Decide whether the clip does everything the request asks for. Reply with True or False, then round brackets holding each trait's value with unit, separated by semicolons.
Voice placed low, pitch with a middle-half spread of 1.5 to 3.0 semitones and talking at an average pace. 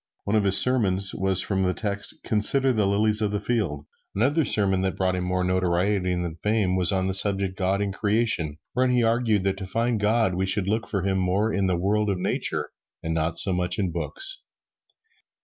False (100 Hz; 2.6 semitones; 210 wpm)